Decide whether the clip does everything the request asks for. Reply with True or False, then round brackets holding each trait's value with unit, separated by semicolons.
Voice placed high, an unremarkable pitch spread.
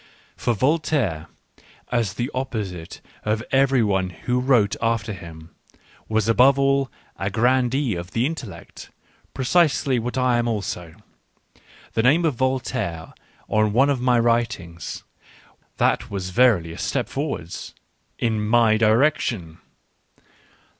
False (115 Hz; 4.9 semitones)